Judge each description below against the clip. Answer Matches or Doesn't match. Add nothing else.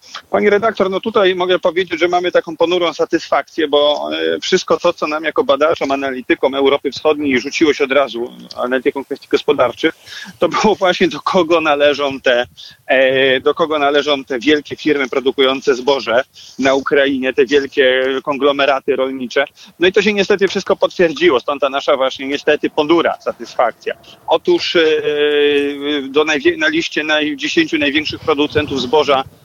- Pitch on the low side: Doesn't match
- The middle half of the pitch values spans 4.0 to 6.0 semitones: Matches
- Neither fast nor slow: Matches